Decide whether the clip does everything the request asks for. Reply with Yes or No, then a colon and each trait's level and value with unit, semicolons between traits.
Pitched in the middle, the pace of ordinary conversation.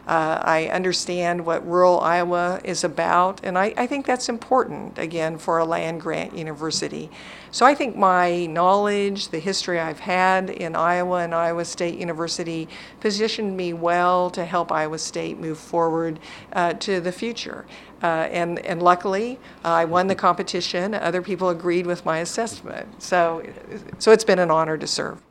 Yes: medium, 175 Hz; average, 170 wpm